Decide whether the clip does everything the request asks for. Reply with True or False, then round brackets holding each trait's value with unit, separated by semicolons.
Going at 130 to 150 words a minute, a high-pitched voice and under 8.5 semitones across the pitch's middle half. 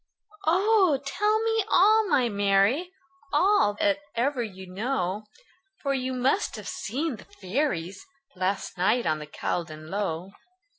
False (140 wpm; 235 Hz; 8.9 semitones)